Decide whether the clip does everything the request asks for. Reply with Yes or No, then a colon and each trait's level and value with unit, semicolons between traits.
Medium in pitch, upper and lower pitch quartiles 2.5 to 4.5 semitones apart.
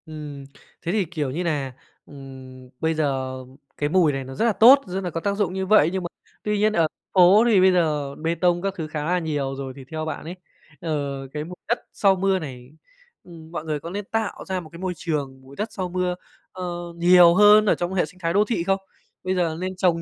Yes: medium, 170 Hz; average, 4.2 semitones